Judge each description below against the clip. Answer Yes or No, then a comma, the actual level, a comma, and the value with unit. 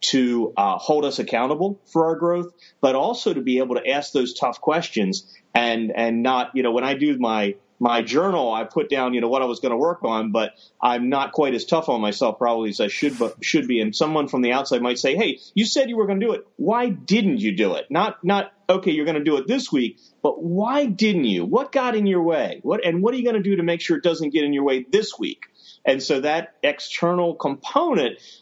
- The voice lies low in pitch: No, medium, 155 Hz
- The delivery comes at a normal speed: No, fast, 255 wpm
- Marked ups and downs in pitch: Yes, wide, 7.9 semitones